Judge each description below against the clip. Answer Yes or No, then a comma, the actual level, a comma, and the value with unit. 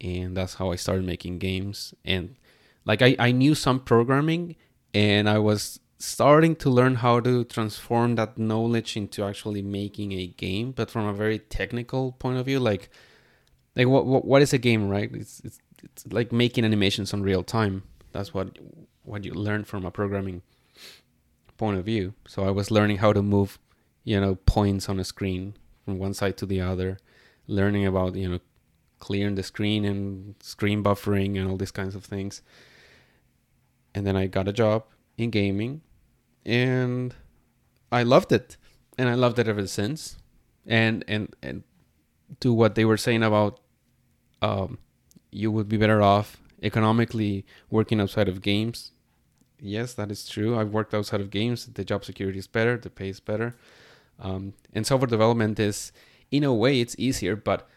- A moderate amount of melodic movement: Yes, average, 3.2 semitones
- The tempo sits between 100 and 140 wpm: No, average, 175 wpm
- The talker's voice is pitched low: Yes, low, 105 Hz